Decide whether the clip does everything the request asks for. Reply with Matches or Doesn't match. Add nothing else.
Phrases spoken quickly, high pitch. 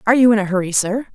Matches